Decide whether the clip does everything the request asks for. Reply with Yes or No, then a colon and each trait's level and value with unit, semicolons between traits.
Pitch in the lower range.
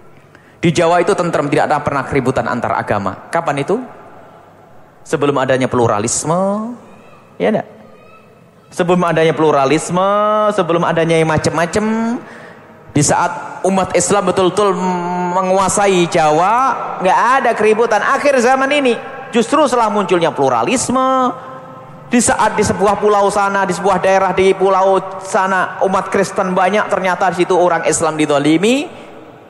No: high, 190 Hz